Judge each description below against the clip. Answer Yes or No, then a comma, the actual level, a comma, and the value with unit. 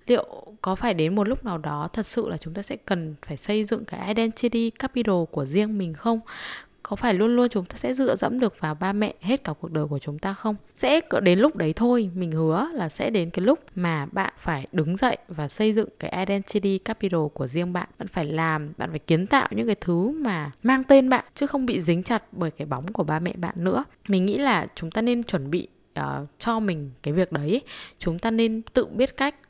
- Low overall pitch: No, high, 195 Hz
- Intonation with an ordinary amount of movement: No, wide, 5.8 semitones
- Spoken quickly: No, average, 240 wpm